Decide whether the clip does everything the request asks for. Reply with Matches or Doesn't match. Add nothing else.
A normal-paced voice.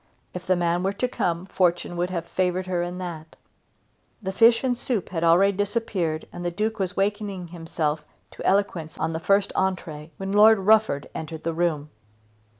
Matches